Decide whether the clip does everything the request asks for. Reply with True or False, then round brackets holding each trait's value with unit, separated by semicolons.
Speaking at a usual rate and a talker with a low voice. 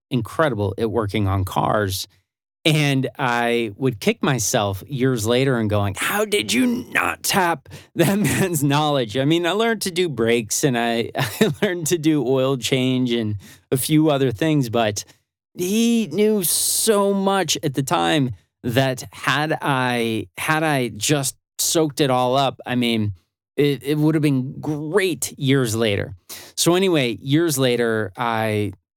True (155 wpm; 130 Hz)